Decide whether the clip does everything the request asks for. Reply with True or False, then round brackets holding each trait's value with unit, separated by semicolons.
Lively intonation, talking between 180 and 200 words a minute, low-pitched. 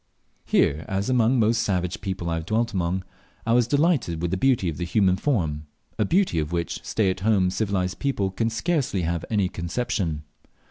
False (5.0 semitones; 190 wpm; 95 Hz)